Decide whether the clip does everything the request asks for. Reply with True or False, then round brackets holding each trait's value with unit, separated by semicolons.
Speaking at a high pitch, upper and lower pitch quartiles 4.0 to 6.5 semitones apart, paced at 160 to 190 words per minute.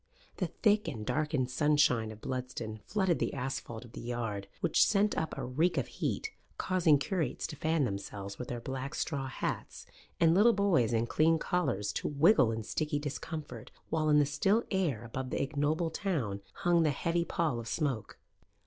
False (145 Hz; 5.6 semitones; 180 wpm)